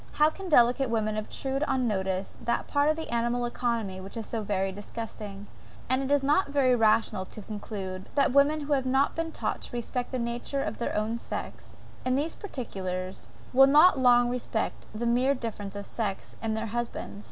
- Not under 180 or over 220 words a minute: Yes, average, 200 wpm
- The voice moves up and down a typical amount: Yes, average, 4.2 semitones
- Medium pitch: No, high, 240 Hz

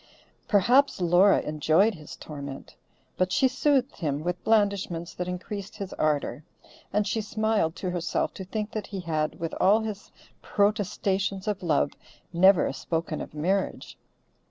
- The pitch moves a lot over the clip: No, average, 4.1 semitones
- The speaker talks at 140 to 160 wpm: Yes, average, 145 wpm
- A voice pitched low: No, high, 190 Hz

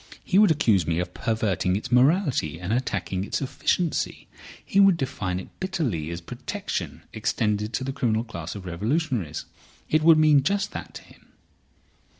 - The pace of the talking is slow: No, average, 160 wpm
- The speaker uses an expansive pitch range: Yes, wide, 8.9 semitones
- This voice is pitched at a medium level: No, low, 115 Hz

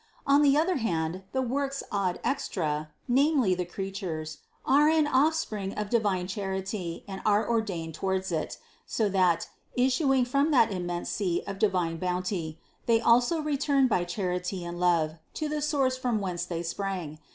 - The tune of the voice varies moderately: No, wide, 6.7 semitones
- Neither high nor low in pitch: No, high, 195 Hz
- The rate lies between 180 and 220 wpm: No, average, 165 wpm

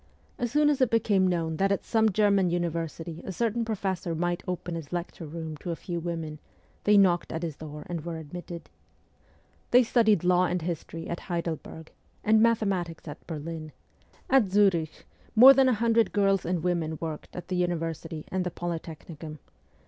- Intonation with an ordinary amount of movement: Yes, average, 3.5 semitones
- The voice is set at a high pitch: No, medium, 175 Hz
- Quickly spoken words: No, average, 175 wpm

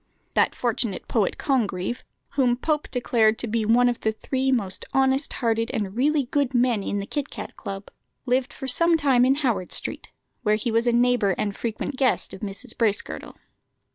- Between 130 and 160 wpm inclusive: No, average, 185 wpm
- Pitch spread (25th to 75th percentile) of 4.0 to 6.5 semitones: No, average, 3.4 semitones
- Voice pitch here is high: Yes, high, 240 Hz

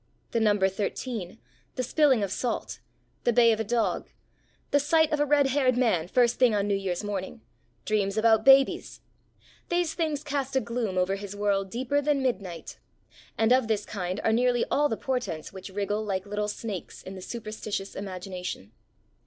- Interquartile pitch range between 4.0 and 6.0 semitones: Yes, average, 4.6 semitones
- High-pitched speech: Yes, high, 220 Hz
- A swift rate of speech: No, average, 175 wpm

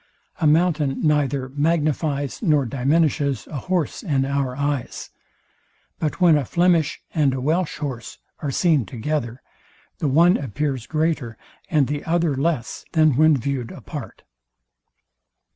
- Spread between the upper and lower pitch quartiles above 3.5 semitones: No, average, 3.1 semitones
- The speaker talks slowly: Yes, slow, 130 wpm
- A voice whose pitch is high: No, medium, 145 Hz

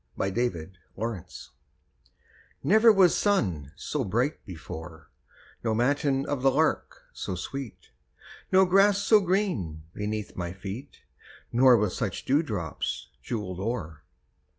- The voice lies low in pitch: Yes, low, 115 Hz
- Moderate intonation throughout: No, wide, 8.3 semitones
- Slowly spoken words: Yes, slow, 120 wpm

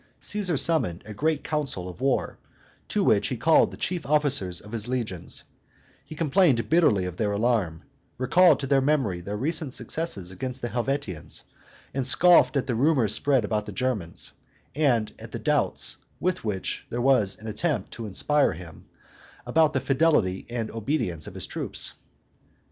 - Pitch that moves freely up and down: Yes, wide, 6.1 semitones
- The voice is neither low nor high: No, low, 125 Hz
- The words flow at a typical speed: Yes, average, 165 wpm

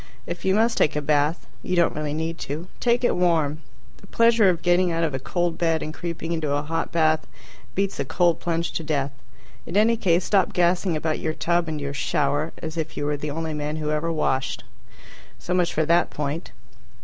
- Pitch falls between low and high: Yes, medium, 165 Hz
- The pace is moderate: No, fast, 215 wpm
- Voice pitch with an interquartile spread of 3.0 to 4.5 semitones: No, narrow, 2.5 semitones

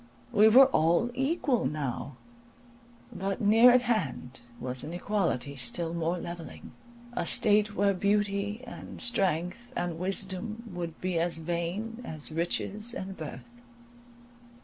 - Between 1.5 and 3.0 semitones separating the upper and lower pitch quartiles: No, average, 4.9 semitones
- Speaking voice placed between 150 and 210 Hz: Yes, high, 190 Hz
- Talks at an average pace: No, slow, 125 wpm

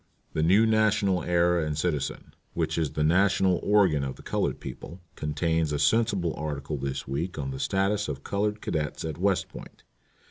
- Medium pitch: No, very low, 85 Hz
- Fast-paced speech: No, average, 175 wpm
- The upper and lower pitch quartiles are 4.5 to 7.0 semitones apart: Yes, average, 4.8 semitones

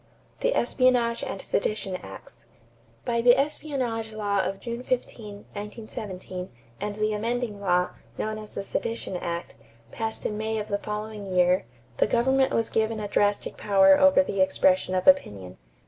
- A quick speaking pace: No, average, 155 wpm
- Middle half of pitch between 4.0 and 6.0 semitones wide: No, average, 3.1 semitones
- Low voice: No, high, 215 Hz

